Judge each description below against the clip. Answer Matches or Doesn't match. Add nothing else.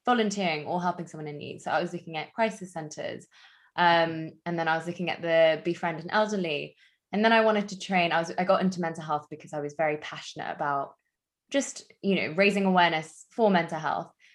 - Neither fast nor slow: Doesn't match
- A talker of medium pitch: Matches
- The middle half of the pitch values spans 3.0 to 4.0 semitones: Matches